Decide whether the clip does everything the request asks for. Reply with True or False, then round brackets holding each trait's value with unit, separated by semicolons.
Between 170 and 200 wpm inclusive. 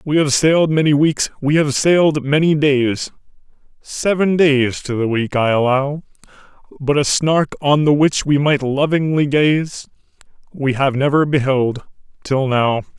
False (155 wpm)